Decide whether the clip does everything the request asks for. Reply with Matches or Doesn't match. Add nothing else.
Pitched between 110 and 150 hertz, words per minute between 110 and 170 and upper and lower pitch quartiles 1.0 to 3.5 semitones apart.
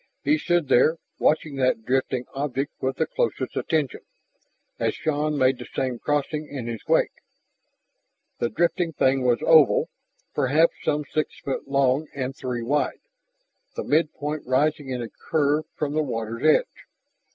Matches